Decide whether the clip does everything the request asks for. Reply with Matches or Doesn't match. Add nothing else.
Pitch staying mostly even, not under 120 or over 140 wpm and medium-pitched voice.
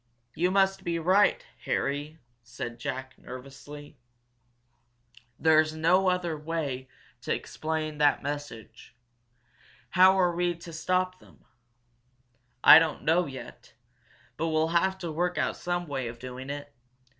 Doesn't match